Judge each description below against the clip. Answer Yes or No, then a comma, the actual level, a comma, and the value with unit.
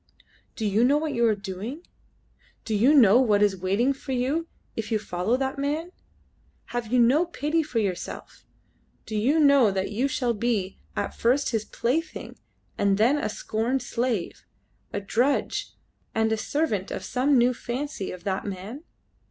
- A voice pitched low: No, high, 240 Hz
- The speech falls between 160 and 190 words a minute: Yes, average, 170 wpm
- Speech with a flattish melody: No, average, 5.0 semitones